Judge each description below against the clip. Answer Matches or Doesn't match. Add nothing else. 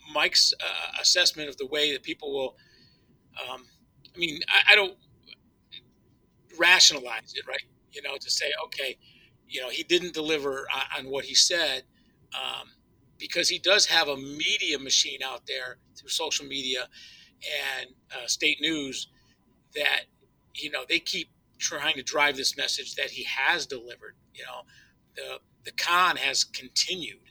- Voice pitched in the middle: Matches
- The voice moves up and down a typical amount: Matches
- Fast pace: Doesn't match